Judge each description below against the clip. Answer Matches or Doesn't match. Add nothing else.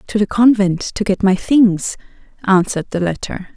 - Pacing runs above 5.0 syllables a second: Doesn't match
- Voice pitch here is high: Matches